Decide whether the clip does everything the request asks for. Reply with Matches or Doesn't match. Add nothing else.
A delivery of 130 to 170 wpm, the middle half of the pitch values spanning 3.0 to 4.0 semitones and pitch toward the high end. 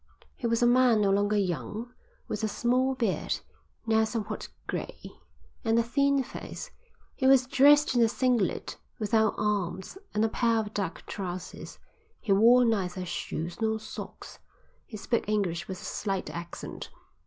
Matches